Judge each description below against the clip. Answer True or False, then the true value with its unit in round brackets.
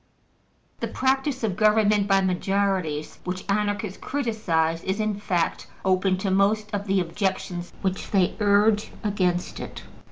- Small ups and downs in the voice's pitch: True (2.3 semitones)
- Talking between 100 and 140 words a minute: True (135 wpm)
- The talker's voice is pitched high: True (195 Hz)